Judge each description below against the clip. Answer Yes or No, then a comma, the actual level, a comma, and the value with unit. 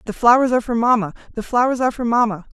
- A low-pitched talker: No, high, 235 Hz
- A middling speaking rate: No, fast, 230 wpm